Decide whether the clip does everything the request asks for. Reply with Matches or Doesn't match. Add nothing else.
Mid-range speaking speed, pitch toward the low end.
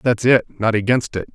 Matches